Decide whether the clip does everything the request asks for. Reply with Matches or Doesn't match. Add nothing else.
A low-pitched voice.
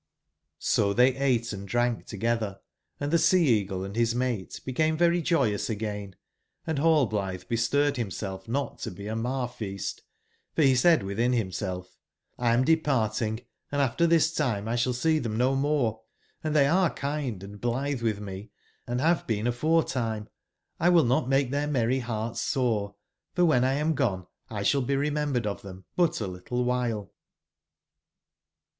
Matches